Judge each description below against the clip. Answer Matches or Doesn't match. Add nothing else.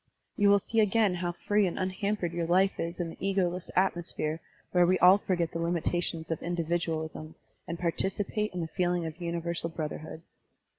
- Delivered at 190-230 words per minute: Doesn't match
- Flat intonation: Matches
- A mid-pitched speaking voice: Matches